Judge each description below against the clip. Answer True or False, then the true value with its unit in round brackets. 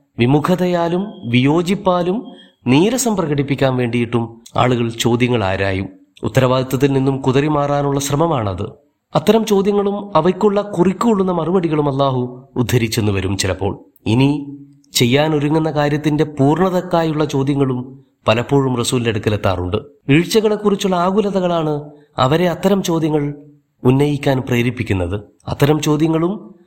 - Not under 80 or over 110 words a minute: True (90 wpm)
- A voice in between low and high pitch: True (145 Hz)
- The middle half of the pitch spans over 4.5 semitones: True (5.4 semitones)